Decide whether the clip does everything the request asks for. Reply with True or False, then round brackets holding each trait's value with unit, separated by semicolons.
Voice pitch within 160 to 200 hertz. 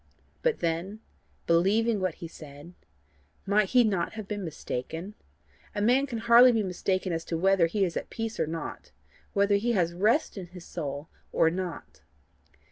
True (190 Hz)